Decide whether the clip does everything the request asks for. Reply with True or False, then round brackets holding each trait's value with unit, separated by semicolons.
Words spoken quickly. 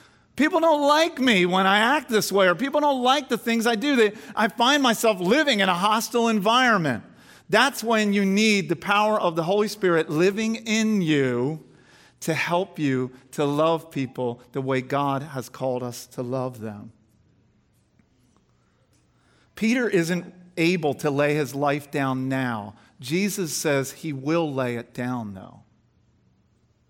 False (160 wpm)